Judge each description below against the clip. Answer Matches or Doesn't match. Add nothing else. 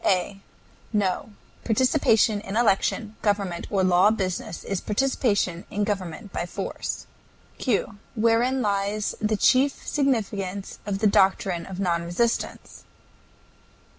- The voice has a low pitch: Doesn't match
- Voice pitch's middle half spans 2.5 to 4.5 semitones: Matches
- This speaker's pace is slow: Matches